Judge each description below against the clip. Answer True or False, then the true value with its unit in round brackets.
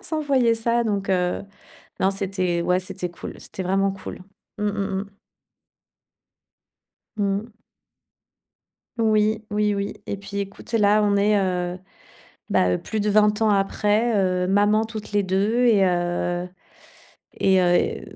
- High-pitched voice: True (200 Hz)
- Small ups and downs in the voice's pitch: True (2.2 semitones)